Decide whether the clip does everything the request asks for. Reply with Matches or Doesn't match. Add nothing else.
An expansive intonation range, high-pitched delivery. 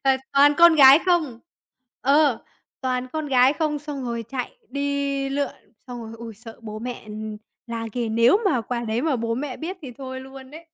Doesn't match